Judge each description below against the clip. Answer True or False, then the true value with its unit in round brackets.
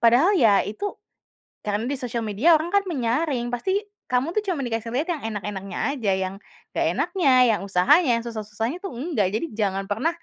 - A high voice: True (240 Hz)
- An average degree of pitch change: False (6.8 semitones)